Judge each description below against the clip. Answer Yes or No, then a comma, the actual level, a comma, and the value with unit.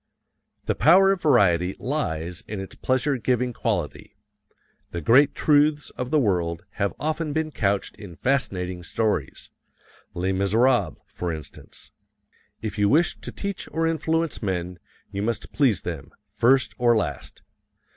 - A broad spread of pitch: Yes, wide, 7.9 semitones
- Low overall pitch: Yes, low, 115 Hz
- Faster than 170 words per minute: No, average, 140 wpm